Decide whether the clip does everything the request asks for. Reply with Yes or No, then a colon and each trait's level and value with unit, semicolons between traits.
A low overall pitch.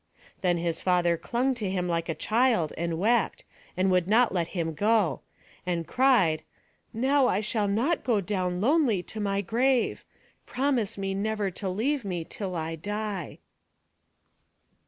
No: high, 200 Hz